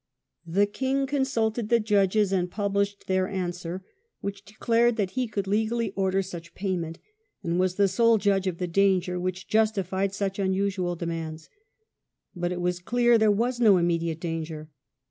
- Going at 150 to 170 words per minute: Yes, average, 165 wpm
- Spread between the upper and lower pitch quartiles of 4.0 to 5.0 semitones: No, average, 3.2 semitones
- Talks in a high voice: Yes, high, 195 Hz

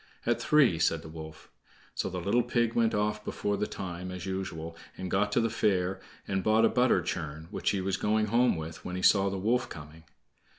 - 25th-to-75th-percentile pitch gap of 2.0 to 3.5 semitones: No, average, 4.0 semitones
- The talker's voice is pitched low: Yes, very low, 95 Hz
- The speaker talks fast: Yes, fast, 215 wpm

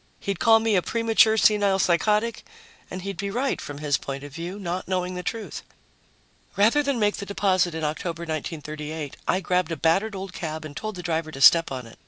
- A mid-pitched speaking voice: Yes, medium, 180 Hz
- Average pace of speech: No, fast, 210 wpm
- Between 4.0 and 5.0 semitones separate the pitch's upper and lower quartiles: Yes, average, 4.6 semitones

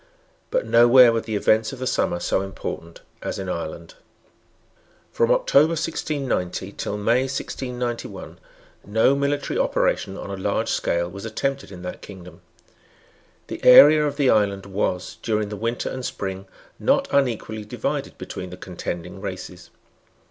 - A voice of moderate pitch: No, low, 110 Hz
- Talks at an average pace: Yes, average, 145 wpm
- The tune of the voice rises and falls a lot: Yes, wide, 5.8 semitones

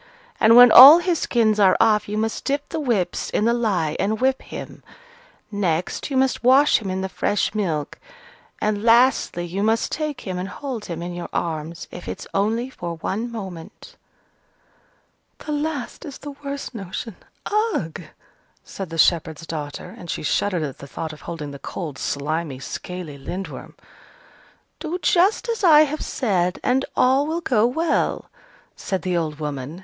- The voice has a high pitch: Yes, high, 205 Hz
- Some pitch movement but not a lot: No, wide, 7.5 semitones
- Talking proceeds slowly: No, average, 170 wpm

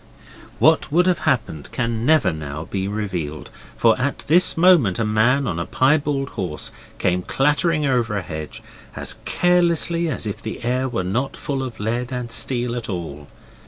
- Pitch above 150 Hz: No, low, 120 Hz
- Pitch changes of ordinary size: No, wide, 6.8 semitones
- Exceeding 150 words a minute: Yes, average, 170 wpm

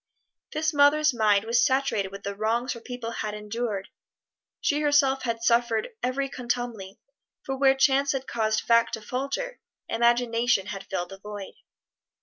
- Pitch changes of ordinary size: Yes, average, 3.8 semitones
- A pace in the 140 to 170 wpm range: Yes, average, 150 wpm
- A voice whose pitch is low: No, high, 235 Hz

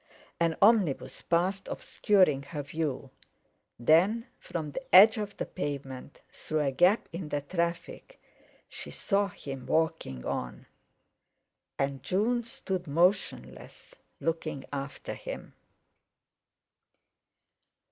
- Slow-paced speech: Yes, slow, 105 wpm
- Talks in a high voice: No, medium, 165 Hz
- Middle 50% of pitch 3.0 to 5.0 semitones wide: No, wide, 5.6 semitones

